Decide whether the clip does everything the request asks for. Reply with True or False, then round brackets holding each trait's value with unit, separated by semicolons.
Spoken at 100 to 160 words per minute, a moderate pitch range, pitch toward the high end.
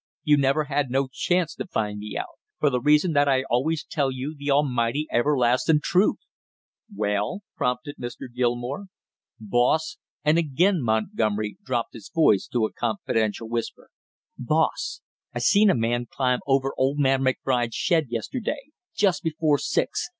False (150 wpm; 4.1 semitones; 135 Hz)